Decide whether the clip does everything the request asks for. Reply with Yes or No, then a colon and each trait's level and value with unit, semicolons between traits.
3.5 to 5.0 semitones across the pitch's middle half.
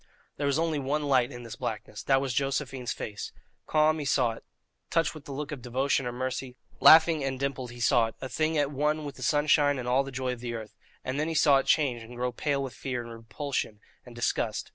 No: average, 3.0 semitones